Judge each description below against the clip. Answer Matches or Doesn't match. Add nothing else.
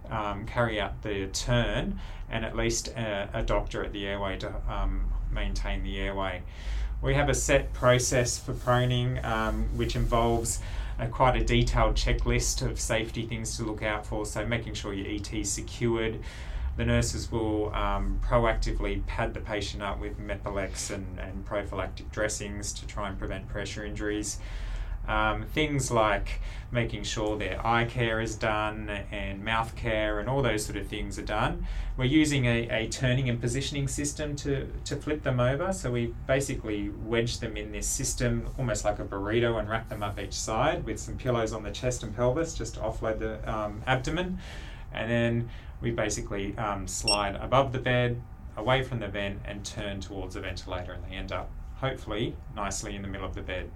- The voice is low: Matches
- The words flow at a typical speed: Matches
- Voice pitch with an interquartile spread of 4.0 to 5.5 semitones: Doesn't match